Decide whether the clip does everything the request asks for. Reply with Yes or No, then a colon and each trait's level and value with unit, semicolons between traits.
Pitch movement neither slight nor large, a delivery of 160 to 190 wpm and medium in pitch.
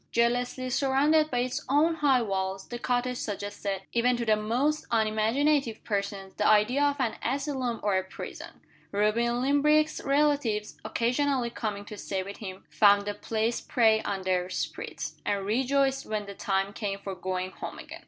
No: average, 4.7 semitones; average, 165 wpm; high, 225 Hz